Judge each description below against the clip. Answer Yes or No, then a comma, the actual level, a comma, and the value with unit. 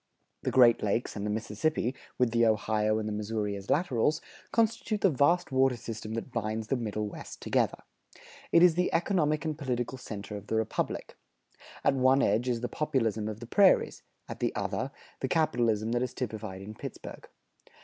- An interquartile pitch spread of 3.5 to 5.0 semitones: Yes, average, 4.3 semitones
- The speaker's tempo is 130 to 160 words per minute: No, average, 180 wpm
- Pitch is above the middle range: No, low, 115 Hz